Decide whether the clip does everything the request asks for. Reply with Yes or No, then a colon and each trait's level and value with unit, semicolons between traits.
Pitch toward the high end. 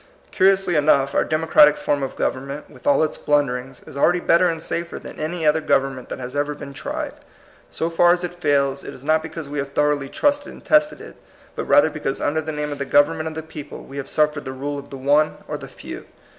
No: medium, 150 Hz